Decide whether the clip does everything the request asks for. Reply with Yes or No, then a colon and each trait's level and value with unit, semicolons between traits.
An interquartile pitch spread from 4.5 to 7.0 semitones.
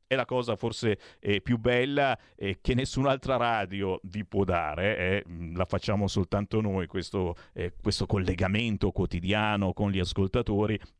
No: average, 2.7 semitones